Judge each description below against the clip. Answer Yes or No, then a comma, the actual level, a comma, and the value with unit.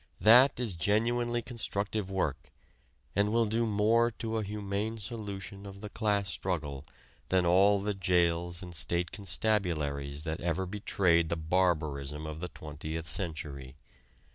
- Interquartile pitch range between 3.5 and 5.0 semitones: Yes, average, 4.5 semitones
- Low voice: Yes, very low, 95 Hz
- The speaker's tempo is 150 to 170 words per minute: No, average, 140 wpm